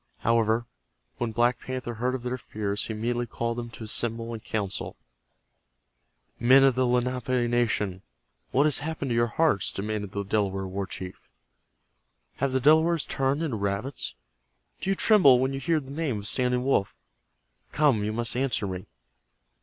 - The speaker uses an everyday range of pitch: Yes, average, 3.7 semitones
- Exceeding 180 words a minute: No, average, 165 wpm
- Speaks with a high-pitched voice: No, low, 120 Hz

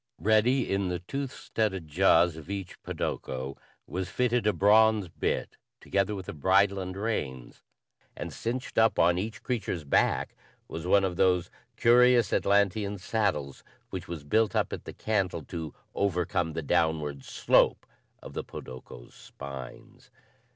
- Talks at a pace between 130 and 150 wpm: Yes, average, 145 wpm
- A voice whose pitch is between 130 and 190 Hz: No, very low, 95 Hz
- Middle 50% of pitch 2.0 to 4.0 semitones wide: No, average, 4.6 semitones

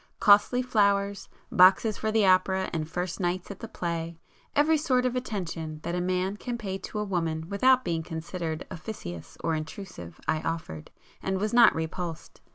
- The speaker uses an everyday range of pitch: Yes, average, 4.3 semitones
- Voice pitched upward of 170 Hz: Yes, medium, 185 Hz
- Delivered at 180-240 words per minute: No, average, 165 wpm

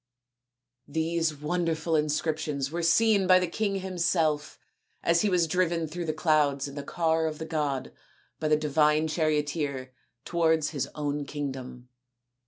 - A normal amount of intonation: No, narrow, 2.3 semitones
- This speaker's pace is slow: No, average, 145 wpm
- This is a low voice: No, medium, 155 Hz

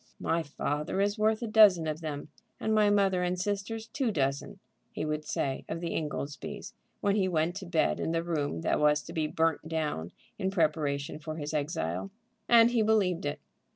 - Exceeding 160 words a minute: Yes, average, 190 wpm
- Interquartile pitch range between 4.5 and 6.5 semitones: Yes, average, 5.1 semitones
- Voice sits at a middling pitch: Yes, medium, 165 Hz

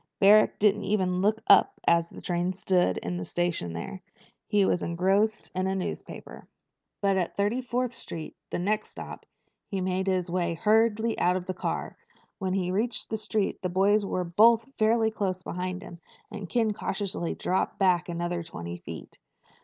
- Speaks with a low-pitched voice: No, high, 190 Hz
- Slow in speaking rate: No, average, 175 wpm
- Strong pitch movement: No, average, 3.2 semitones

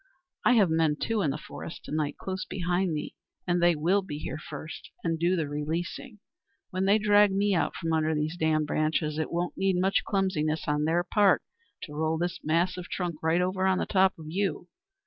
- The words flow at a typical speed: No, fast, 210 wpm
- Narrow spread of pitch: No, average, 3.4 semitones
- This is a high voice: No, medium, 170 Hz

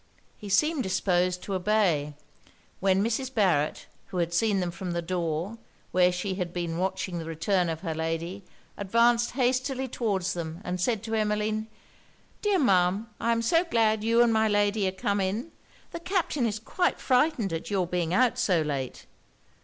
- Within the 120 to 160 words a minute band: No, average, 175 wpm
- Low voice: No, high, 195 Hz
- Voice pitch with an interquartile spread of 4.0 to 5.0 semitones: Yes, average, 4.5 semitones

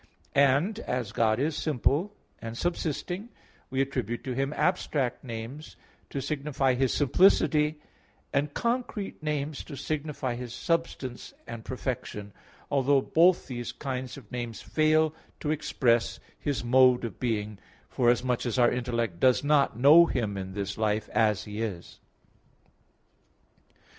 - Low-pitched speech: Yes, low, 130 Hz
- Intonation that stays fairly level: No, average, 4.3 semitones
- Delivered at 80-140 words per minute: Yes, slow, 135 wpm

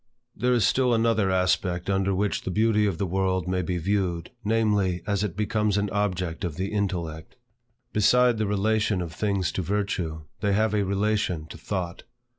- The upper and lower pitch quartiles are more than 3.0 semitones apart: No, narrow, 2.6 semitones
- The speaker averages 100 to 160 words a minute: No, average, 180 wpm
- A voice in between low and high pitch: No, low, 100 Hz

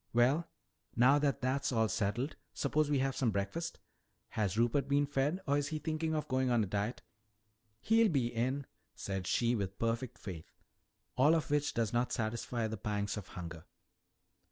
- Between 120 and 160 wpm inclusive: No, average, 180 wpm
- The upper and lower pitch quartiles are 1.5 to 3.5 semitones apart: No, average, 4.8 semitones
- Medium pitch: No, low, 125 Hz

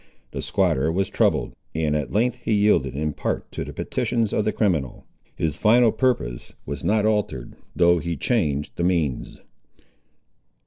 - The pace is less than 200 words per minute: Yes, average, 160 wpm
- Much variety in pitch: Yes, wide, 6.5 semitones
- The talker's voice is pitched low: Yes, very low, 85 Hz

